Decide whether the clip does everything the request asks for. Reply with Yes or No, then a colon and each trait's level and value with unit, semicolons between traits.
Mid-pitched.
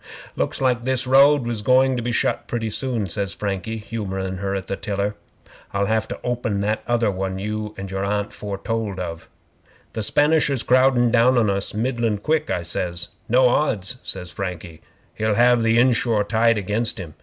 No: low, 110 Hz